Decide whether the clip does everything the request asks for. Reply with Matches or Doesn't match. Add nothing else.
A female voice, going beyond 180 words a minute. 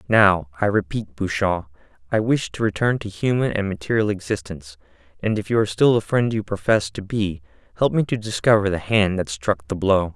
Doesn't match